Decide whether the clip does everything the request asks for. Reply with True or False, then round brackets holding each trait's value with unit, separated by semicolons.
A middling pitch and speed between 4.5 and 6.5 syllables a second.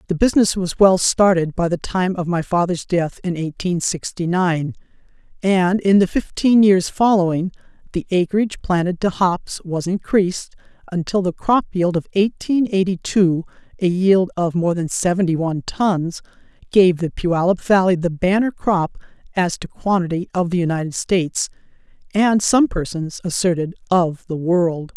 True (180 Hz; 4.6 syllables/s)